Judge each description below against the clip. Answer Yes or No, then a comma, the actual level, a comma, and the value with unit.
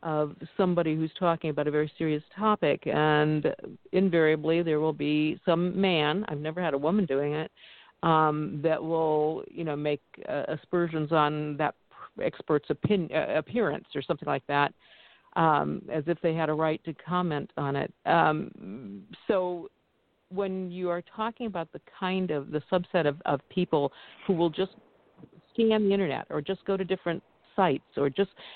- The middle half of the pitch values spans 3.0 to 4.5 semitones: Yes, average, 3.3 semitones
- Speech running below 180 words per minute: Yes, average, 165 wpm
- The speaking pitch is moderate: Yes, medium, 160 Hz